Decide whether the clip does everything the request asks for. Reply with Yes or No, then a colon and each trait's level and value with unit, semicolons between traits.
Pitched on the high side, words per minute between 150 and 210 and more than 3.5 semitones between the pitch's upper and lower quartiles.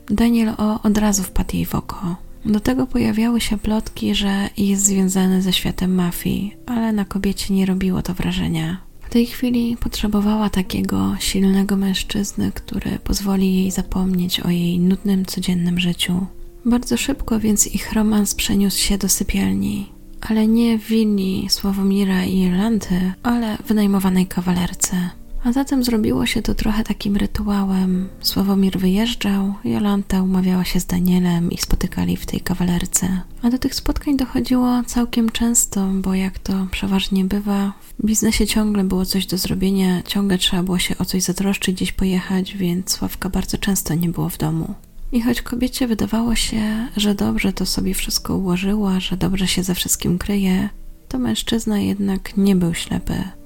No: high, 195 Hz; fast, 160 wpm; average, 2.8 semitones